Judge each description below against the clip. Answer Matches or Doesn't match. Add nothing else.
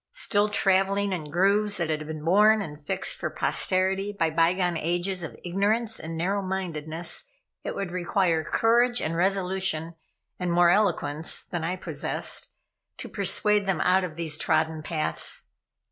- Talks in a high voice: Doesn't match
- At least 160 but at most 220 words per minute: Doesn't match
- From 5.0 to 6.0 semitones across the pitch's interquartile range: Doesn't match